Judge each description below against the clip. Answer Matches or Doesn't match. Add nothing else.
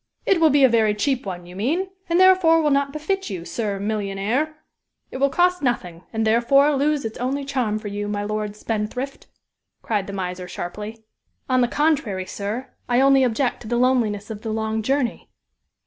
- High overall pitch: Matches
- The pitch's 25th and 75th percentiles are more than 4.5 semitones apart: Matches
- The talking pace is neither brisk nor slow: Matches